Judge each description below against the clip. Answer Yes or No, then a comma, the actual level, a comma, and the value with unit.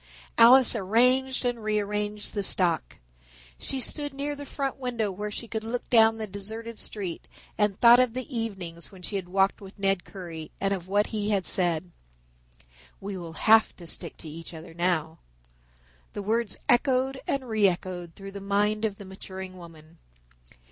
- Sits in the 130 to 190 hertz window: No, high, 205 Hz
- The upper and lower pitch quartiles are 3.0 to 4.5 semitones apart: Yes, average, 3.8 semitones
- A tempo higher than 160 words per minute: Yes, average, 175 wpm